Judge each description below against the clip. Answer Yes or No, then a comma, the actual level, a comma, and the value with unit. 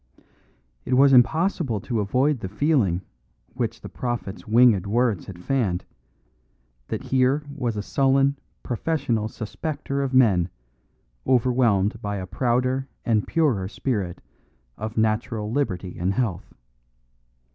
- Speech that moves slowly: Yes, slow, 120 wpm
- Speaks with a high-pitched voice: No, low, 120 Hz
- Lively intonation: No, average, 4.6 semitones